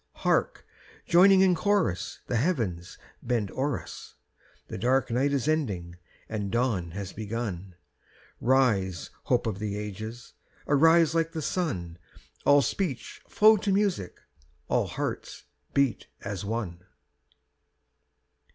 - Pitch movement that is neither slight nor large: No, wide, 8.1 semitones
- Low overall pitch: Yes, low, 120 Hz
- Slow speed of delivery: Yes, slow, 120 wpm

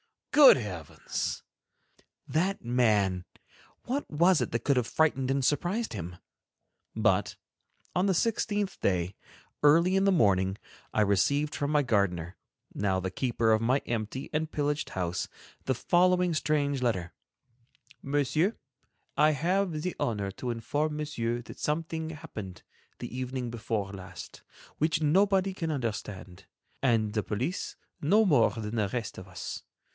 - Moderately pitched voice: No, low, 130 Hz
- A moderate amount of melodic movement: No, wide, 7.2 semitones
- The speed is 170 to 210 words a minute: No, average, 140 wpm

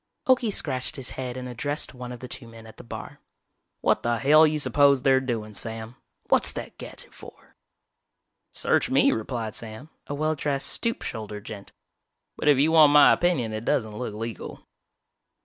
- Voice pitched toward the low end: Yes, low, 125 Hz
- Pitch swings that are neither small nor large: Yes, average, 4.5 semitones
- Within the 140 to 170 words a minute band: No, average, 180 wpm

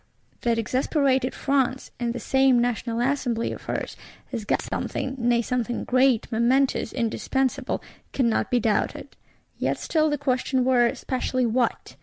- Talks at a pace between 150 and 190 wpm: No, average, 140 wpm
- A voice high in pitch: Yes, very high, 250 Hz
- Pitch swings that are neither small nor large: No, narrow, 2.0 semitones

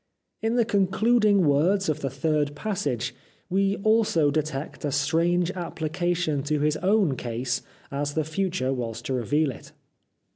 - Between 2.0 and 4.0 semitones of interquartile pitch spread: No, average, 5.3 semitones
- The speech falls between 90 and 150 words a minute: Yes, average, 145 wpm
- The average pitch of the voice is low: No, medium, 155 Hz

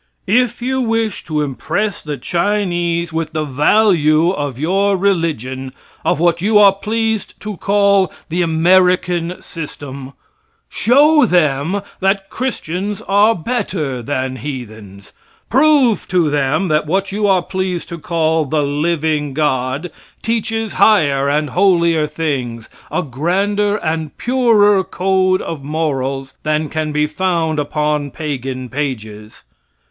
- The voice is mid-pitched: Yes, medium, 165 Hz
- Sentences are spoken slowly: Yes, slow, 125 wpm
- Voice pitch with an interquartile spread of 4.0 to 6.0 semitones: Yes, average, 5.3 semitones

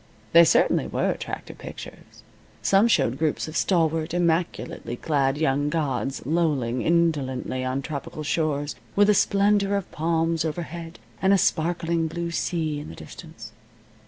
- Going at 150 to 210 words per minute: No, average, 140 wpm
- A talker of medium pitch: Yes, medium, 160 Hz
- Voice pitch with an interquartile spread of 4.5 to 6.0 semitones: No, average, 2.9 semitones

